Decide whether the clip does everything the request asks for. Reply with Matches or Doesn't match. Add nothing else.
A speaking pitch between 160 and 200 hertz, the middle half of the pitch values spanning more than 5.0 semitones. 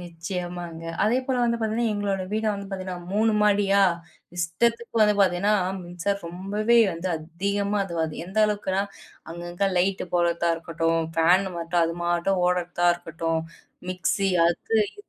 Doesn't match